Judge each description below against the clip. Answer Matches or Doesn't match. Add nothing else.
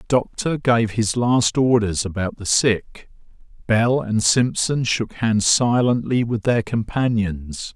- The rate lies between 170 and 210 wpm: Doesn't match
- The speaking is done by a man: Matches